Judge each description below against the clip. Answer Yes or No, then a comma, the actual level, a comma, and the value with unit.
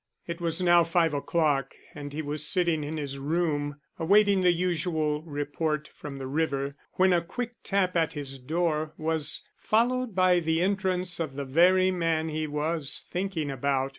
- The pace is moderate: Yes, average, 165 wpm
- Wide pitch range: No, average, 3.4 semitones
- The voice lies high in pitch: No, medium, 160 Hz